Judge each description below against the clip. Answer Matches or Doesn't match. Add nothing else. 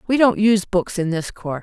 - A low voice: Doesn't match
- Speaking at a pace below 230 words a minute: Doesn't match